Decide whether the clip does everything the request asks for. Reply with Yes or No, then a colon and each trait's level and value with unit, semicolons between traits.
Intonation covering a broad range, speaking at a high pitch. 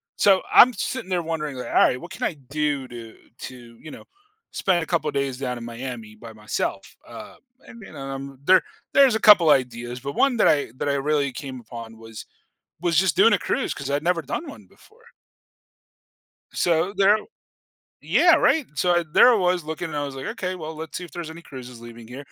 No: wide, 6.0 semitones; medium, 150 Hz